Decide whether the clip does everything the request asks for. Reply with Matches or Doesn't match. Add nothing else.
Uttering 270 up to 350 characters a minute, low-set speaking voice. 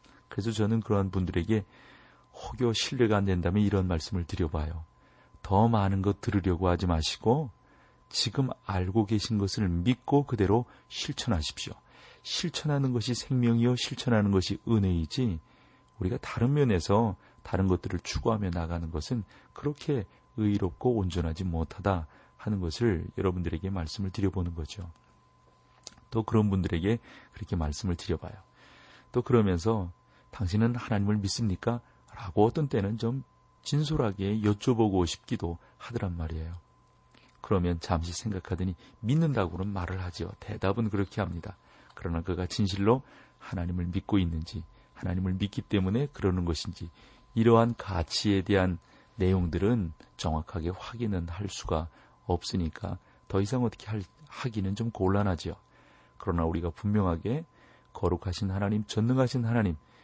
Matches